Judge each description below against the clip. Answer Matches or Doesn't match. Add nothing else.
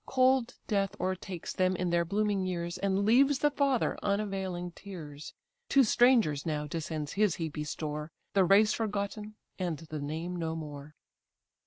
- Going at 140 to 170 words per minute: Matches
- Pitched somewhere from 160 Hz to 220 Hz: Matches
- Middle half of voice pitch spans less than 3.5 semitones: Doesn't match